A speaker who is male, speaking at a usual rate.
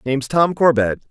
Yes: male; average, 165 wpm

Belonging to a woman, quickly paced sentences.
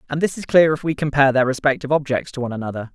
No: male; fast, 265 wpm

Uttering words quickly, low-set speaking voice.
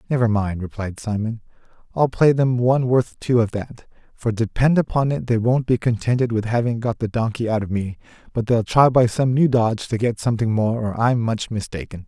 Yes: fast, 215 wpm; low, 115 Hz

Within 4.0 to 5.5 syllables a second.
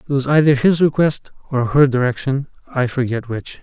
Yes: 5.1 syllables/s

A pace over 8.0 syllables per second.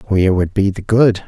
No: 5.6 syllables/s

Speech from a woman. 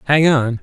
No: male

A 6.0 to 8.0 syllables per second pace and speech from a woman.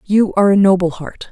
No: 5.8 syllables/s; female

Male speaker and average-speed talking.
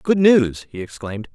Yes: male; average, 180 wpm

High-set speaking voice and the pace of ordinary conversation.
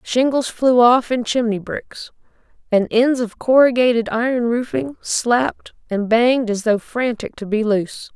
Yes: high, 235 Hz; average, 155 wpm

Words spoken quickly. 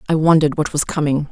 Yes: fast, 230 wpm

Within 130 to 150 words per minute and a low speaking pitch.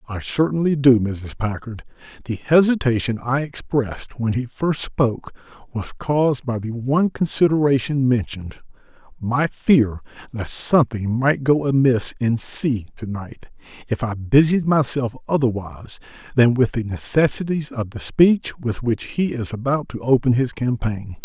Yes: average, 145 wpm; low, 125 Hz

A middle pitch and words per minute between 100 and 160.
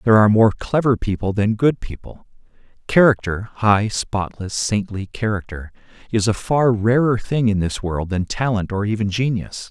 No: low, 110 Hz; average, 150 wpm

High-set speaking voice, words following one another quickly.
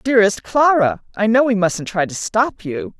No: high, 215 Hz; average, 180 wpm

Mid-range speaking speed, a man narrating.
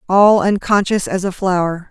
No: average, 155 wpm; female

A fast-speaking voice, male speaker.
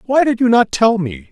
Yes: fast, 275 wpm; male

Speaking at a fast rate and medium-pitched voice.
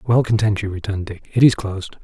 No: fast, 235 wpm; low, 105 Hz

